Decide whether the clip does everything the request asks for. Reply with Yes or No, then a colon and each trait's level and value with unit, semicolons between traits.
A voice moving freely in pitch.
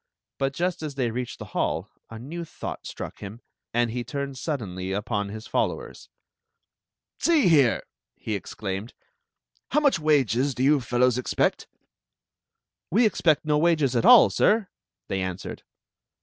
Yes: wide, 5.8 semitones